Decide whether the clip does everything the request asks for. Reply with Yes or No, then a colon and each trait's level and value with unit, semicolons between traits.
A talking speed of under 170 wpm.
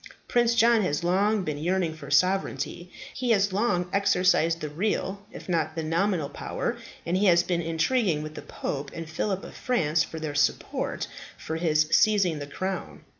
No: average, 175 wpm